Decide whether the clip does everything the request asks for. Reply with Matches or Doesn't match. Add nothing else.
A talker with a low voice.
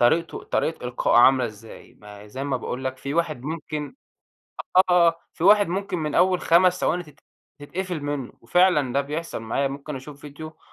Doesn't match